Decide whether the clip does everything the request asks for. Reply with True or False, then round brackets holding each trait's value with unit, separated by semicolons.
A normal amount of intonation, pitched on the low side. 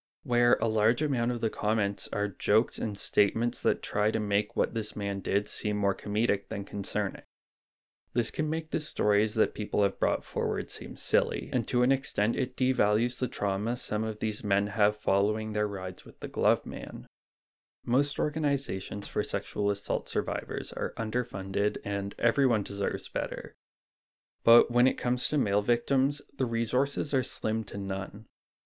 True (3.2 semitones; 110 Hz)